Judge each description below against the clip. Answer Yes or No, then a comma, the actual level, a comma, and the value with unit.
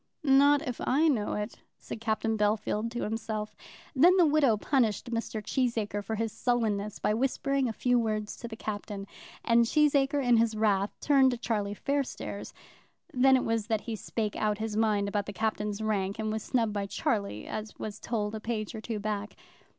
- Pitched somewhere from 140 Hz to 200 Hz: No, high, 220 Hz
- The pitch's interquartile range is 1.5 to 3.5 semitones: Yes, average, 2.8 semitones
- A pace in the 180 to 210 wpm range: Yes, average, 190 wpm